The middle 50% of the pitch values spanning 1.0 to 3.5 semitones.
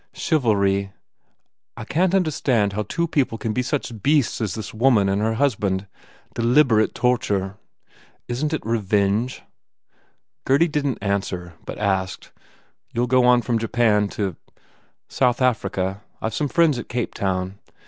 No: average, 4.5 semitones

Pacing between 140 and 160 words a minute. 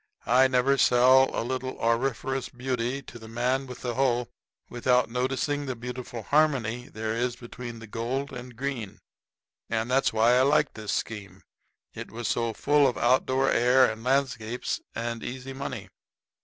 Yes: average, 155 wpm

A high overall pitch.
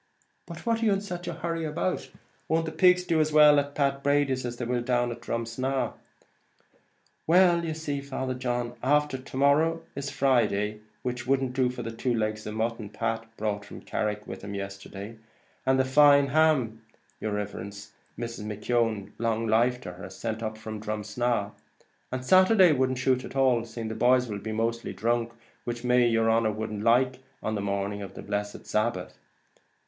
No: low, 120 Hz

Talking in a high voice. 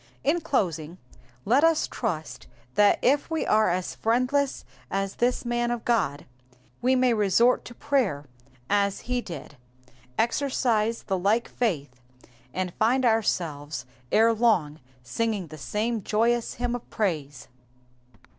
Yes: high, 220 Hz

